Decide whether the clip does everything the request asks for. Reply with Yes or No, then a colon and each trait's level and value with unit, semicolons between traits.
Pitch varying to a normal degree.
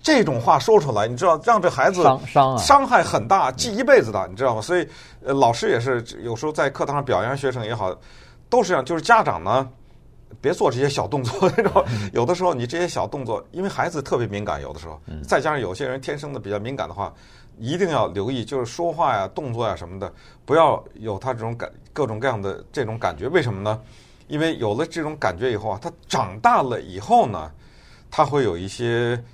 No: wide, 6.5 semitones